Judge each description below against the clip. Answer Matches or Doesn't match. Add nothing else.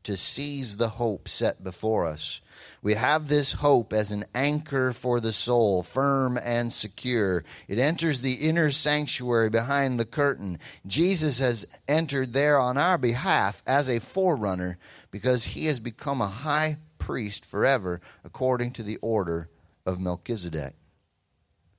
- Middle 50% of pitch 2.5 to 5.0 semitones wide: Doesn't match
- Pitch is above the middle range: Doesn't match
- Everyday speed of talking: Matches